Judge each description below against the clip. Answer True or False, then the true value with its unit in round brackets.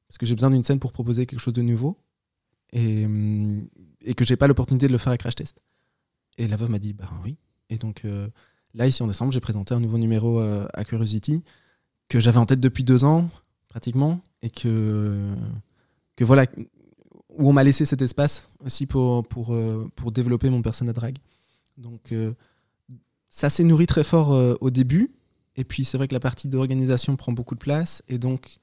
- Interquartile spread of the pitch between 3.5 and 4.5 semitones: False (2.8 semitones)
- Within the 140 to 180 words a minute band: False (205 wpm)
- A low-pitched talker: True (125 Hz)